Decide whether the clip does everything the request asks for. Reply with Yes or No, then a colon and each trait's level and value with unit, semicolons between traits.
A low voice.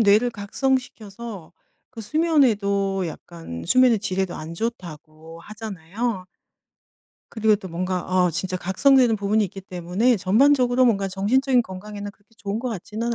No: high, 205 Hz